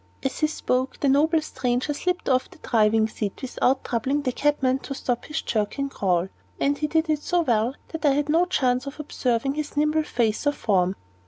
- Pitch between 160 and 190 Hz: No, very high, 270 Hz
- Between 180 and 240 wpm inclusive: Yes, average, 200 wpm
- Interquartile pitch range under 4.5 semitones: Yes, average, 3.9 semitones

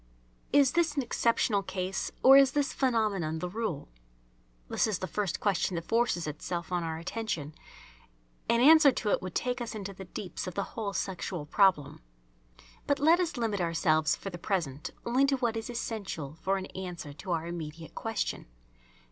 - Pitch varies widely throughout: Yes, wide, 5.8 semitones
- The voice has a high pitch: Yes, high, 195 Hz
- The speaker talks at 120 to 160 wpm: No, average, 180 wpm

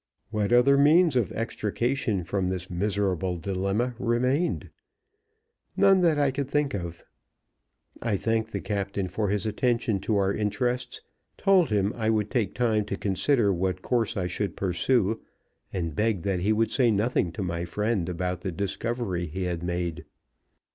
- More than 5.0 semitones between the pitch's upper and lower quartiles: No, average, 4.5 semitones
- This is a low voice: Yes, low, 105 Hz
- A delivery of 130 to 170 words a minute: Yes, average, 160 wpm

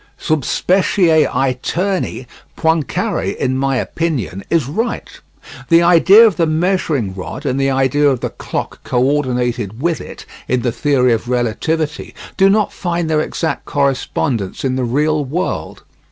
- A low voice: No, medium, 145 Hz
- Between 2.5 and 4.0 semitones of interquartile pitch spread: No, average, 4.6 semitones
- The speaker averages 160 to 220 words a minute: No, average, 150 wpm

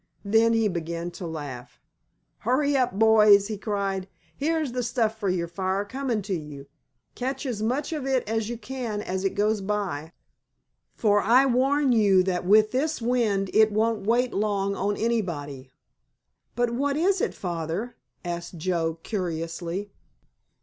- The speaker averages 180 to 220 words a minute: No, average, 155 wpm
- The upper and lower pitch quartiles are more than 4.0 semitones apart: Yes, average, 4.6 semitones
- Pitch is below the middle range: No, high, 210 Hz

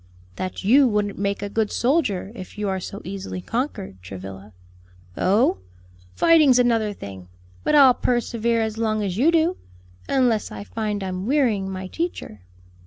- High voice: Yes, high, 210 Hz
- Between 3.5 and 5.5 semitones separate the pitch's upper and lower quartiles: Yes, average, 4.6 semitones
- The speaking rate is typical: Yes, average, 155 wpm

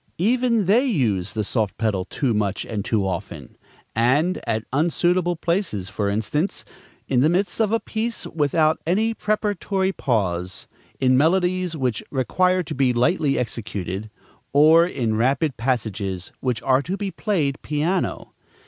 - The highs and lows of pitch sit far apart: Yes, wide, 8.7 semitones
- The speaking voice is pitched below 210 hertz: Yes, medium, 140 Hz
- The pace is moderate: Yes, average, 145 wpm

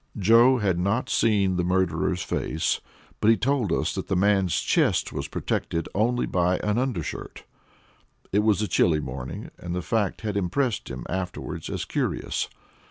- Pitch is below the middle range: Yes, low, 100 Hz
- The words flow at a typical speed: Yes, average, 165 wpm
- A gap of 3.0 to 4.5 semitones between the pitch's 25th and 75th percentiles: Yes, average, 3.8 semitones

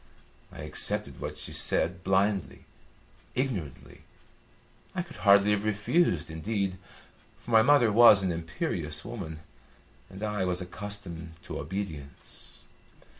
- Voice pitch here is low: Yes, low, 100 Hz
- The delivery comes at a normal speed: No, slow, 120 wpm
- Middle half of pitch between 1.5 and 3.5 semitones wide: No, average, 4.0 semitones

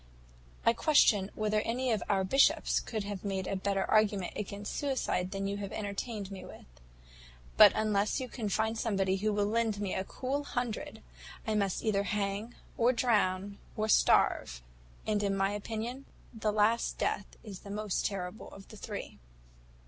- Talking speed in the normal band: Yes, average, 165 wpm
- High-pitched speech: Yes, high, 205 Hz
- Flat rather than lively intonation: Yes, narrow, 2.2 semitones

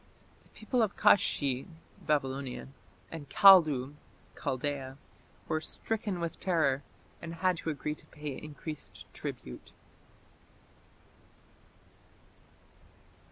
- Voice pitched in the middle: Yes, medium, 150 Hz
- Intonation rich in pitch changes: No, average, 3.8 semitones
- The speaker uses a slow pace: Yes, slow, 90 wpm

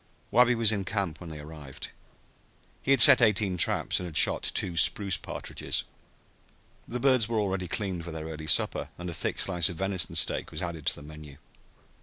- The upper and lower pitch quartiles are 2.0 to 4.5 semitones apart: No, average, 4.9 semitones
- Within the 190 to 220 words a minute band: Yes, average, 195 wpm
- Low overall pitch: Yes, very low, 90 Hz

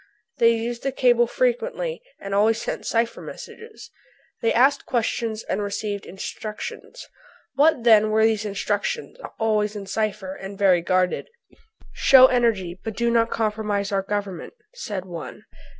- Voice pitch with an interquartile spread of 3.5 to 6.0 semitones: No, average, 3.0 semitones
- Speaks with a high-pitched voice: Yes, high, 220 Hz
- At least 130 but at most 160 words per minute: Yes, average, 140 wpm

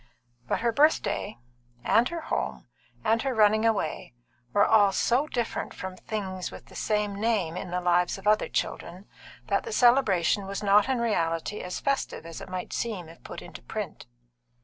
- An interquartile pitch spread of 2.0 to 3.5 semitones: No, average, 4.1 semitones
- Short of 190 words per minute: Yes, average, 175 wpm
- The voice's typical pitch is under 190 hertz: No, high, 210 Hz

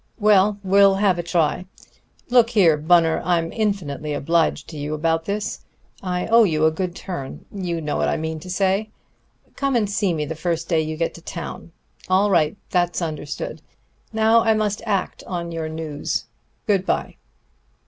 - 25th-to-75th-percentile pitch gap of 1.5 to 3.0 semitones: No, average, 3.8 semitones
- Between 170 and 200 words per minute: Yes, average, 175 wpm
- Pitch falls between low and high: Yes, medium, 175 Hz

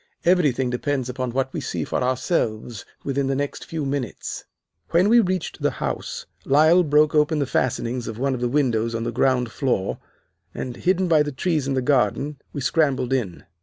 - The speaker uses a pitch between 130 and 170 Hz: Yes, low, 135 Hz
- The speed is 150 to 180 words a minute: No, average, 190 wpm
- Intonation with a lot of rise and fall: No, average, 3.3 semitones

